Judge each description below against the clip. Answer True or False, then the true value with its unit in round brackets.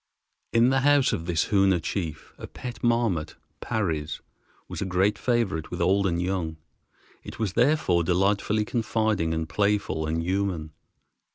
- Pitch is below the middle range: True (95 Hz)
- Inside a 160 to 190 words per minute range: False (150 wpm)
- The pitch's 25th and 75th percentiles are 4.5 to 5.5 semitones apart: True (4.9 semitones)